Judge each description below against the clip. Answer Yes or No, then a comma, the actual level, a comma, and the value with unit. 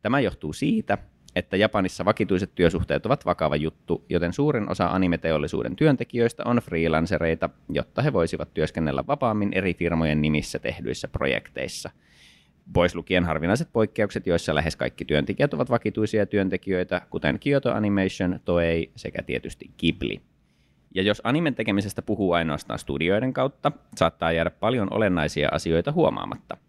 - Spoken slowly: No, average, 135 wpm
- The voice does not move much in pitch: No, average, 4.5 semitones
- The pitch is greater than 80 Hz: Yes, very low, 95 Hz